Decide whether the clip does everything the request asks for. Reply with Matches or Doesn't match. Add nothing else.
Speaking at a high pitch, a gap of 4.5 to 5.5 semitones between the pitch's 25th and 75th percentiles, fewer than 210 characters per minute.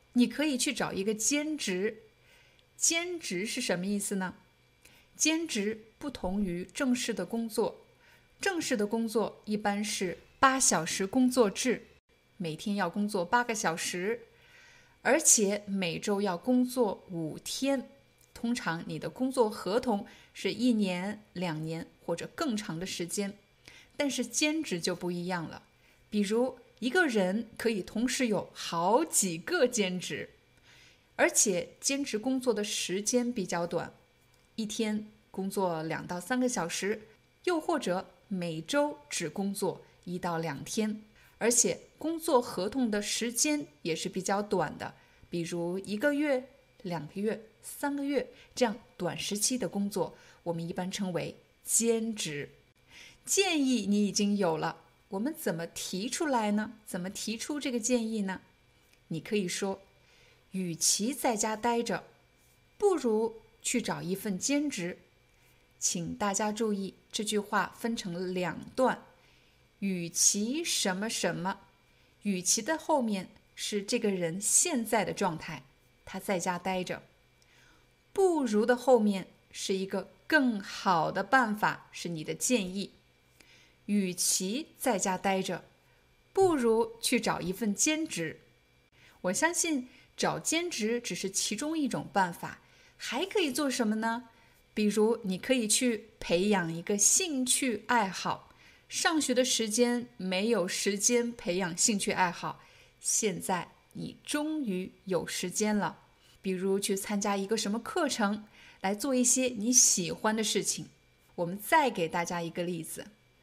Matches